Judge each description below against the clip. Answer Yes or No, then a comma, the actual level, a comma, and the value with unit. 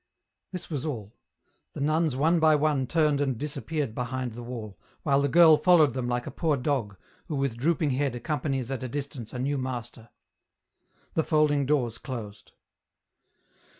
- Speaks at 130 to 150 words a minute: No, average, 170 wpm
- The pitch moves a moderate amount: Yes, average, 3.7 semitones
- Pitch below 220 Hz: Yes, medium, 140 Hz